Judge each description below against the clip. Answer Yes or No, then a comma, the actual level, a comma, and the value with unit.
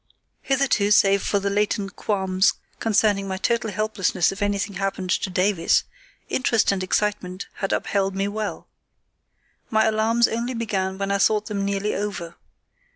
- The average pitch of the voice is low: No, high, 200 Hz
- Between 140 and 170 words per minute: Yes, average, 150 wpm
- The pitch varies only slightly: Yes, narrow, 1.8 semitones